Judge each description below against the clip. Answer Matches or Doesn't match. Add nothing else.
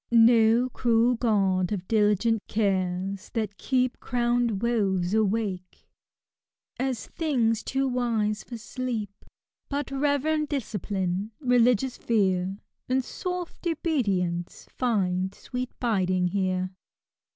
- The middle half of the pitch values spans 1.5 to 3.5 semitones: Doesn't match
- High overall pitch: Matches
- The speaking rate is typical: Doesn't match